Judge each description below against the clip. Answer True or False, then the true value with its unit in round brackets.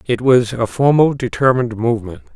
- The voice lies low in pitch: True (125 Hz)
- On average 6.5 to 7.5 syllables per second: False (6.1 syllables/s)